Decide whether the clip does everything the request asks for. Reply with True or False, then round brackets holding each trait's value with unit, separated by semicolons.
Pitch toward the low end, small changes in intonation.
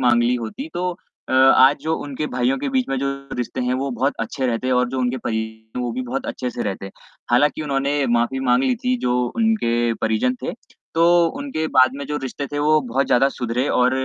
False (130 Hz; 3.0 semitones)